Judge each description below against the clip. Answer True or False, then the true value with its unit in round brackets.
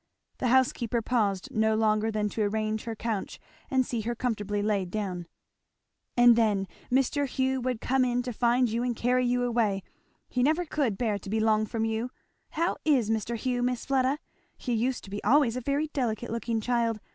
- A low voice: False (235 Hz)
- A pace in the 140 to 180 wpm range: False (190 wpm)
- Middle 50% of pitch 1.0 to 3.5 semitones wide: True (2.7 semitones)